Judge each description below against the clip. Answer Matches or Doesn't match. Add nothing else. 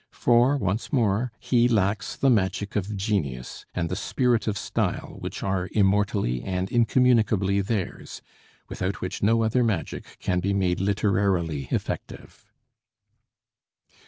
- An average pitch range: Matches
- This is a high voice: Doesn't match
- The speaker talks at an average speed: Doesn't match